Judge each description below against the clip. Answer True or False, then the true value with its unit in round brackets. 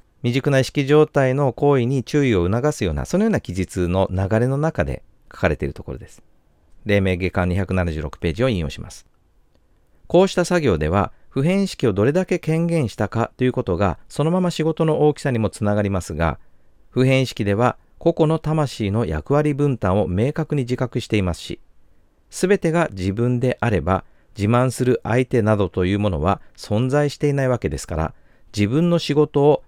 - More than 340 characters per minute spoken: True (350 characters per minute)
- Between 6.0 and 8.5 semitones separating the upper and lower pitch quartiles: True (7.9 semitones)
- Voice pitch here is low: True (120 Hz)